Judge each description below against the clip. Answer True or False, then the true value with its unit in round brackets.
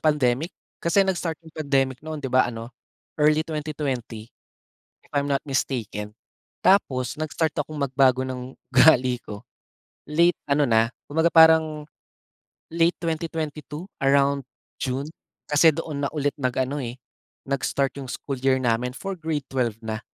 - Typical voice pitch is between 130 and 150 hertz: True (140 Hz)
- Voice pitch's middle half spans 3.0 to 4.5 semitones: True (3.5 semitones)